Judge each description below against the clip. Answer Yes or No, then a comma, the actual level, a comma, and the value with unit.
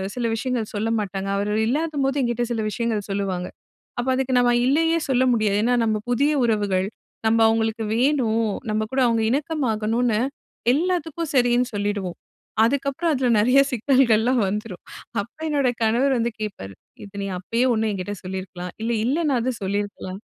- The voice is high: Yes, high, 230 Hz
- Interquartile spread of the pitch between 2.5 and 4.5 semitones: Yes, average, 4.2 semitones